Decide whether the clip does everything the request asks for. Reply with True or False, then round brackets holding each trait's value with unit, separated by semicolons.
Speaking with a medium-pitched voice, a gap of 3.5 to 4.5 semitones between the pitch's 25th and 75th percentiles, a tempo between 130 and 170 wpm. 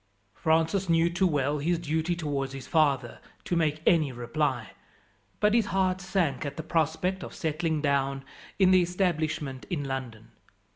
True (160 Hz; 4.0 semitones; 155 wpm)